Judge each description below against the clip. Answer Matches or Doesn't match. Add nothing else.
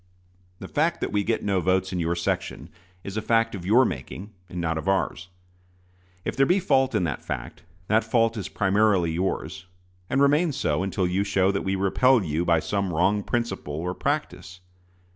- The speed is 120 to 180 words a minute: Doesn't match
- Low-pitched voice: Matches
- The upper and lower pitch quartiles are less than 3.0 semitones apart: Doesn't match